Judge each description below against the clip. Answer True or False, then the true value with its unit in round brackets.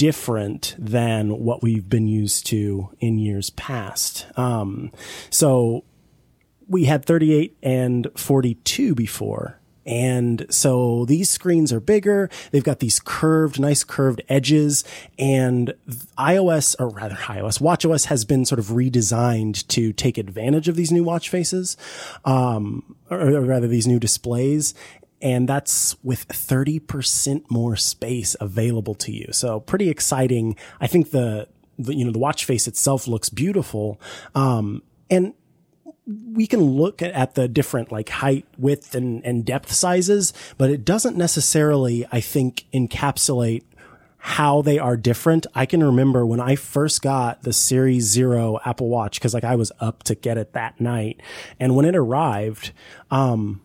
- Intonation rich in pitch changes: False (4.1 semitones)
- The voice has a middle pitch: False (130 Hz)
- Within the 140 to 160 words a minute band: True (150 wpm)